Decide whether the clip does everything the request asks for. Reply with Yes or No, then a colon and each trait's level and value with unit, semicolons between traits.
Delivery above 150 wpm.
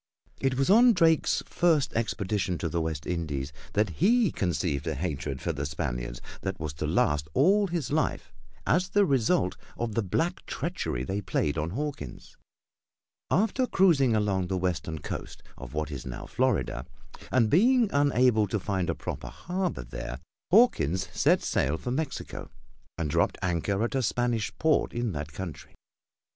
Yes: average, 160 wpm